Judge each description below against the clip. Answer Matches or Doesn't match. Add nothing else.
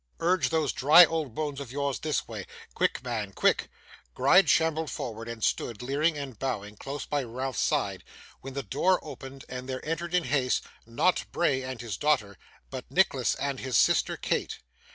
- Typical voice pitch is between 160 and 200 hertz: Doesn't match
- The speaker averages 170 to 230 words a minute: Matches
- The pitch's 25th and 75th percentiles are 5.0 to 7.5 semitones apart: Doesn't match